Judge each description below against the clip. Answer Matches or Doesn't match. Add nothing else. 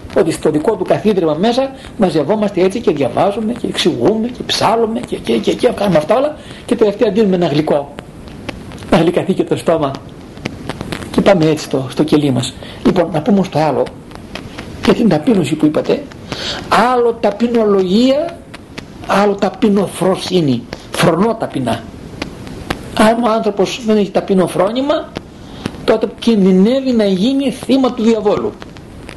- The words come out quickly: Doesn't match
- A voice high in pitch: Matches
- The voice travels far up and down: Doesn't match